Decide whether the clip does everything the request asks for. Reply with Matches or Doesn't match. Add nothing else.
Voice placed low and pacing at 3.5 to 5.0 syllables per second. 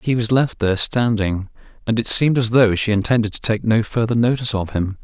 Doesn't match